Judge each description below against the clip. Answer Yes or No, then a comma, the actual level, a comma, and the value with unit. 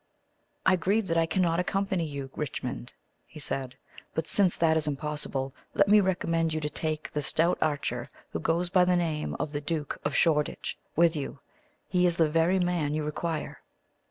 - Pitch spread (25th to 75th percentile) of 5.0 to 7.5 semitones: No, average, 2.9 semitones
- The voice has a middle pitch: Yes, medium, 160 Hz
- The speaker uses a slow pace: No, average, 185 wpm